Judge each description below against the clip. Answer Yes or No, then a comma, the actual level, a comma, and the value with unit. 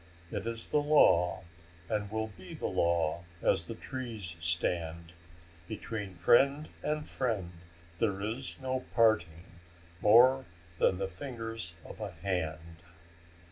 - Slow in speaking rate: Yes, slow, 125 wpm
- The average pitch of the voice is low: Yes, low, 100 Hz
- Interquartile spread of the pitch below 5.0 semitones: No, wide, 5.5 semitones